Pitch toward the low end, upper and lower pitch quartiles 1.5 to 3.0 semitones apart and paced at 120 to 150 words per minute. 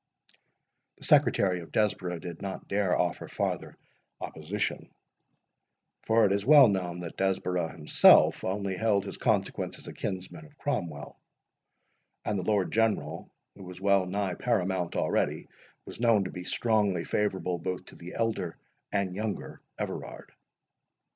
Yes: very low, 95 Hz; average, 2.7 semitones; average, 140 wpm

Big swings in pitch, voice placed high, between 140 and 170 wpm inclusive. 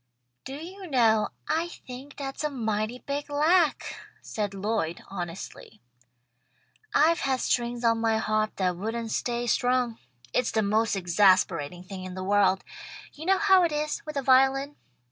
Yes: wide, 5.8 semitones; high, 235 Hz; average, 155 wpm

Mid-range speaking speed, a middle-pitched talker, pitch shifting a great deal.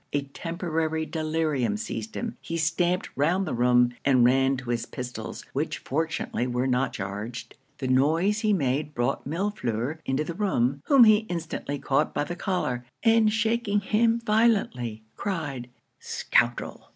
Yes: average, 150 wpm; medium, 155 Hz; wide, 7.5 semitones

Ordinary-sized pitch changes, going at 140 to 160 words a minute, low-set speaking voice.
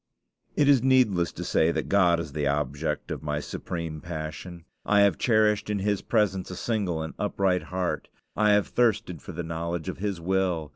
No: average, 4.1 semitones; average, 190 wpm; very low, 90 Hz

